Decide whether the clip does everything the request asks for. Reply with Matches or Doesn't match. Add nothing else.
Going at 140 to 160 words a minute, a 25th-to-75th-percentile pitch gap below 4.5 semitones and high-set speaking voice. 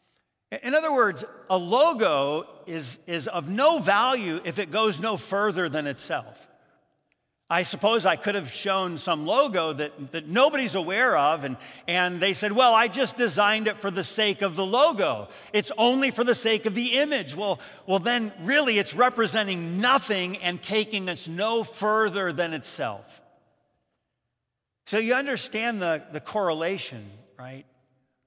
Doesn't match